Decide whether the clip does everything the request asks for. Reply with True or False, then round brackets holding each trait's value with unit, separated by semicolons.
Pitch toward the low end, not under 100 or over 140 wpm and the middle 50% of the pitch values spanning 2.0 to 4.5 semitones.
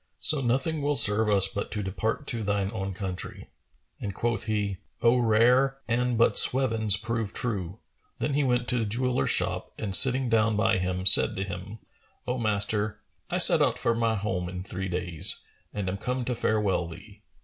False (110 Hz; 185 wpm; 3.8 semitones)